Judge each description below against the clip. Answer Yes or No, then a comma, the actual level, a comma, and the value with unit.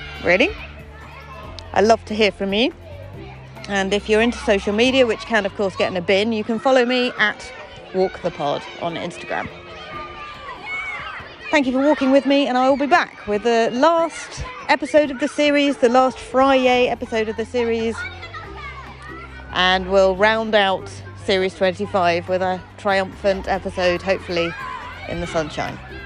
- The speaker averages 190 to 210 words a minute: No, average, 160 wpm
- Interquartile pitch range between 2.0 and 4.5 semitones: No, average, 5.3 semitones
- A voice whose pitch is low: No, high, 210 Hz